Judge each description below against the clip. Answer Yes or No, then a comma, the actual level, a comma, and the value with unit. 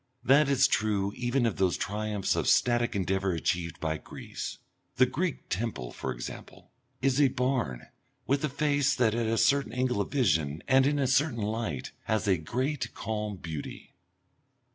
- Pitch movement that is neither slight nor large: No, wide, 5.7 semitones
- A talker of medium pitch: No, low, 115 Hz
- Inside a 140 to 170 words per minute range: Yes, average, 165 wpm